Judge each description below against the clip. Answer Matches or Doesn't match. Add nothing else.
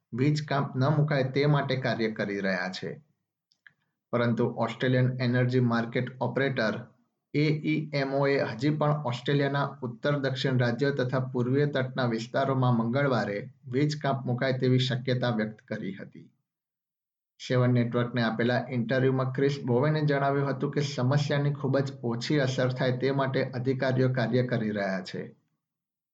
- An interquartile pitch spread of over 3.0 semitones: Doesn't match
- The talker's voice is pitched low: Matches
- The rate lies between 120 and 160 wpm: Matches